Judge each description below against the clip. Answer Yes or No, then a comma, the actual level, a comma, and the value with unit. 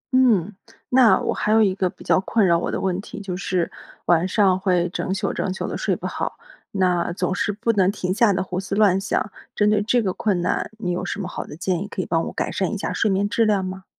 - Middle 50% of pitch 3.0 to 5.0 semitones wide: No, narrow, 2.4 semitones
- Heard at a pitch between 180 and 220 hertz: Yes, high, 190 Hz